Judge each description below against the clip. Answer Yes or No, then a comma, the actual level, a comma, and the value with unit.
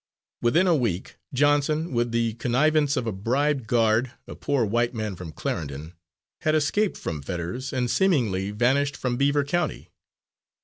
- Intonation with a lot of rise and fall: No, average, 5.0 semitones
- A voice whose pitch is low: Yes, low, 125 Hz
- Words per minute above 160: No, average, 150 wpm